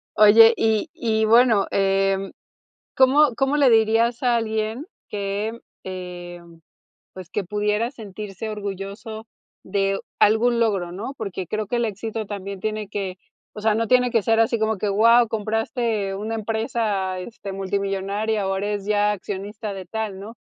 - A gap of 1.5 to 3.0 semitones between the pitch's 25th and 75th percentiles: Yes, narrow, 2.4 semitones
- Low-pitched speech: No, high, 210 Hz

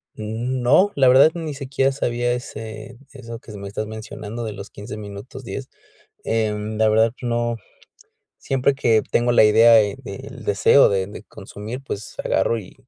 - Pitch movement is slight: No, average, 3.1 semitones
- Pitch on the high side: No, low, 115 Hz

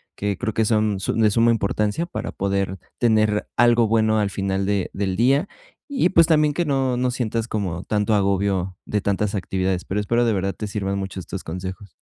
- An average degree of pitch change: Yes, average, 3.0 semitones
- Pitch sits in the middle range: No, low, 105 Hz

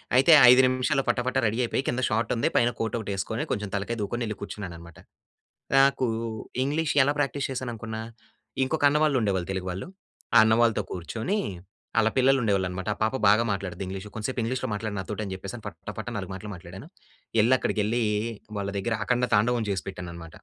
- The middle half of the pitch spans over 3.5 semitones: Yes, average, 4.4 semitones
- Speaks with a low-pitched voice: Yes, low, 110 Hz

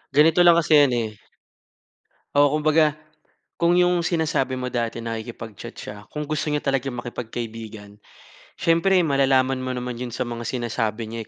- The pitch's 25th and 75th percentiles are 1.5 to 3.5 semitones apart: No, average, 4.8 semitones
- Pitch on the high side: No, low, 130 Hz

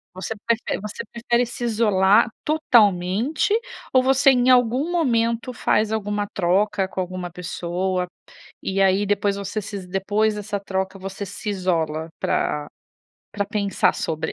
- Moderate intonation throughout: Yes, average, 3.7 semitones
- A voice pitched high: Yes, high, 205 Hz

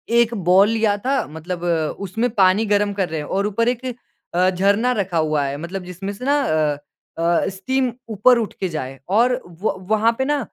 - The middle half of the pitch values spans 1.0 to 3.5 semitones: No, average, 5.0 semitones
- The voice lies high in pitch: Yes, high, 200 Hz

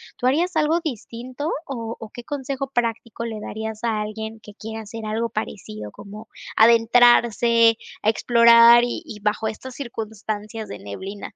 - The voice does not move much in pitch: Yes, narrow, 1.9 semitones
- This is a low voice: No, high, 225 Hz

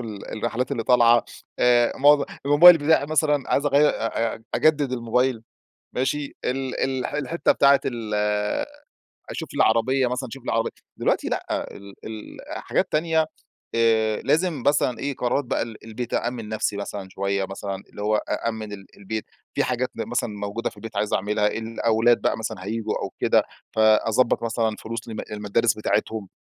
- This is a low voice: Yes, low, 115 Hz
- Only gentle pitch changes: No, average, 3.6 semitones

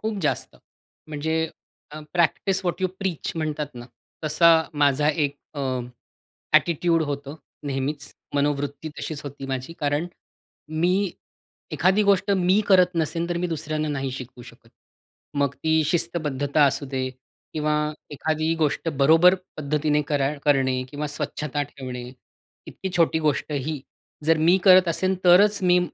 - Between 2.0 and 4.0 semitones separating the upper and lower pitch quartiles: Yes, average, 3.3 semitones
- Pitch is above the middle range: No, medium, 155 Hz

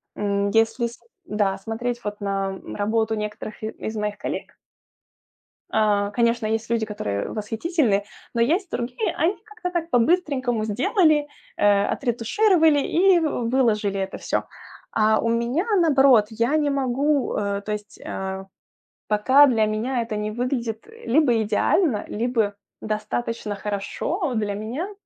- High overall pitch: Yes, high, 230 Hz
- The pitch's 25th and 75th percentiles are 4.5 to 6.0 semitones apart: Yes, average, 4.8 semitones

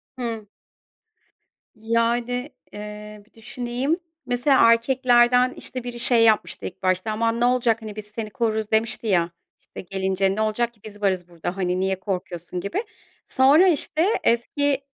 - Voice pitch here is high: Yes, high, 225 Hz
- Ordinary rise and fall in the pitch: Yes, average, 3.3 semitones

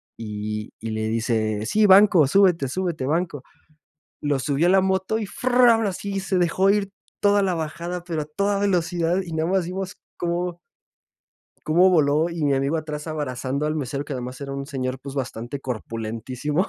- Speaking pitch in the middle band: Yes, medium, 160 Hz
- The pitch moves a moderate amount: No, wide, 5.8 semitones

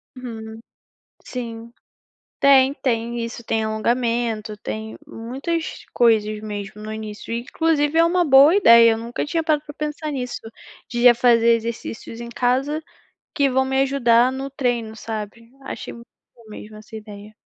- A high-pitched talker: Yes, high, 235 Hz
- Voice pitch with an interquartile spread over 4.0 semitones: No, average, 3.4 semitones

